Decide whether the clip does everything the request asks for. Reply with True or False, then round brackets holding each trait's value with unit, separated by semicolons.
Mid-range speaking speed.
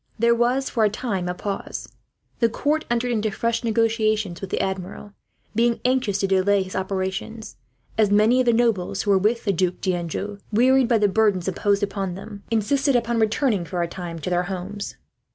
True (190 wpm)